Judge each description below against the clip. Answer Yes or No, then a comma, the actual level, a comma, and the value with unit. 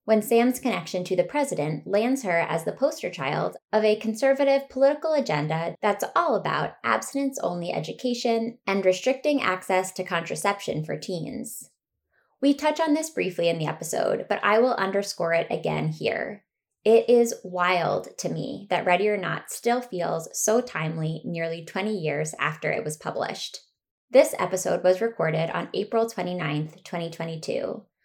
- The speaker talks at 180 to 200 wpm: No, average, 155 wpm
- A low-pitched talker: No, high, 190 Hz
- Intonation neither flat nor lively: No, wide, 6.1 semitones